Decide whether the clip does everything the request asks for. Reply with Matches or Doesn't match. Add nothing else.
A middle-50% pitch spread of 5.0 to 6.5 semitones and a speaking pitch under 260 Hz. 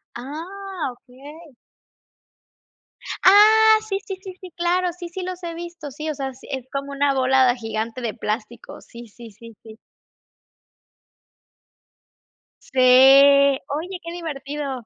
Doesn't match